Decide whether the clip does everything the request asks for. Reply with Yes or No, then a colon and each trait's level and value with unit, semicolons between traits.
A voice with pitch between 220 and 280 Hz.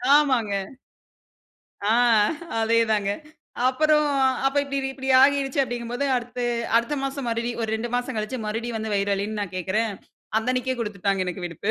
Yes: high, 235 Hz